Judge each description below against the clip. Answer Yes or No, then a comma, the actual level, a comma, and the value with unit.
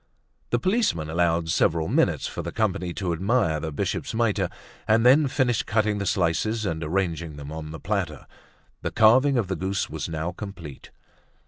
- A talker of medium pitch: No, very low, 95 Hz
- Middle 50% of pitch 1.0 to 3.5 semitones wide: No, wide, 5.5 semitones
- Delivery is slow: No, average, 175 wpm